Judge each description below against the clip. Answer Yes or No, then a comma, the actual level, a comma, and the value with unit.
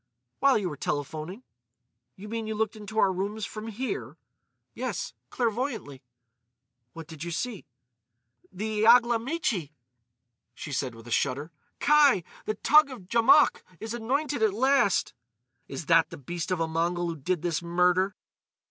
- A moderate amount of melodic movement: No, wide, 5.9 semitones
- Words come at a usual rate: Yes, average, 150 wpm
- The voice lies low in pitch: No, high, 200 Hz